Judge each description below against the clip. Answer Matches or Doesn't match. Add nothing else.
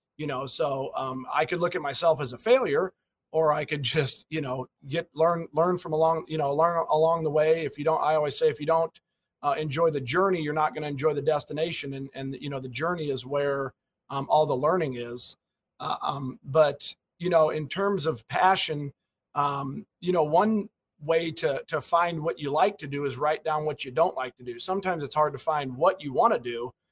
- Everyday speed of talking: Doesn't match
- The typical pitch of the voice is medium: Matches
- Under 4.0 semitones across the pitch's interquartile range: Matches